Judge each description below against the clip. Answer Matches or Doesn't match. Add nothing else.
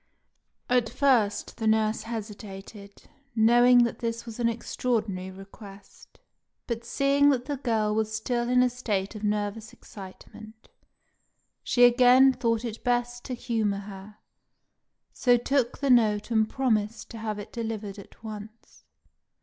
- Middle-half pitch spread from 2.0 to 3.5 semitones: Matches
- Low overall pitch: Doesn't match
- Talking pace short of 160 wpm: Matches